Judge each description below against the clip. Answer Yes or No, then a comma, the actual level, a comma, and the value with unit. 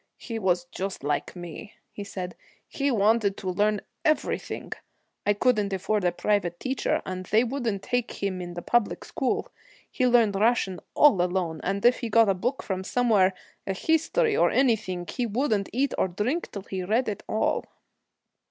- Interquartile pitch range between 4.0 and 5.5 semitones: Yes, average, 4.5 semitones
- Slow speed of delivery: No, average, 175 wpm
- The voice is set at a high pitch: Yes, high, 205 Hz